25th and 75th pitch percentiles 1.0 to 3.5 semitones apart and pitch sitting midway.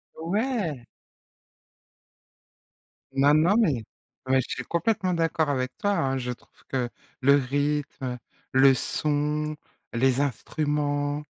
Yes: average, 3.2 semitones; medium, 145 Hz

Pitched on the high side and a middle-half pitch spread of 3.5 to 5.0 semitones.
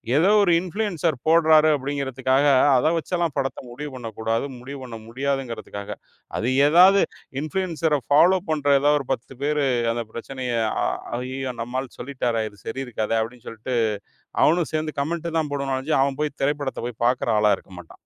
No: low, 135 Hz; average, 4.1 semitones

